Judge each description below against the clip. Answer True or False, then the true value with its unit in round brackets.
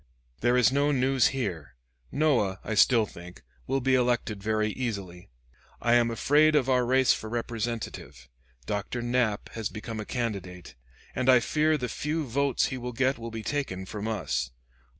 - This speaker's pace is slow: False (170 wpm)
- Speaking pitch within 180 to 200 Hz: False (120 Hz)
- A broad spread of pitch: False (3.7 semitones)